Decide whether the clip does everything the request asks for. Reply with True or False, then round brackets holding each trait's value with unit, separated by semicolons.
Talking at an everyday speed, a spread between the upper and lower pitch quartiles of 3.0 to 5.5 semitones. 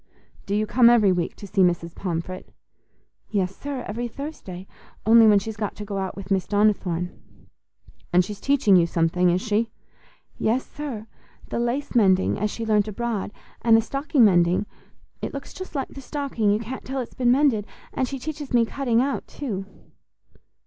True (175 wpm; 4.6 semitones)